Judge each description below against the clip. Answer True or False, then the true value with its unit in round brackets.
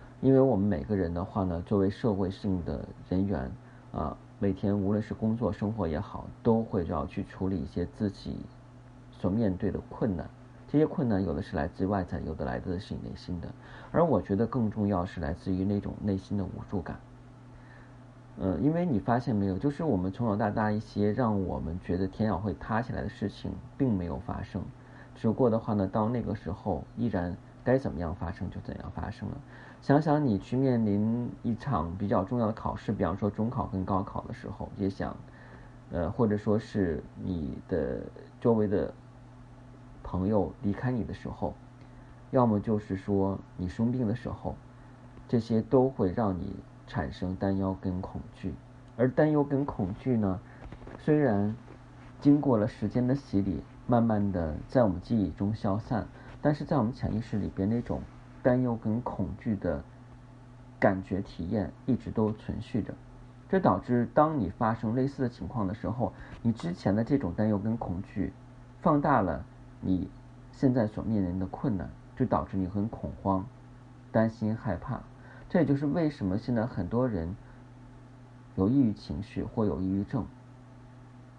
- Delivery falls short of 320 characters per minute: True (255 characters per minute)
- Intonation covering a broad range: False (4.3 semitones)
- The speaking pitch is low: True (110 Hz)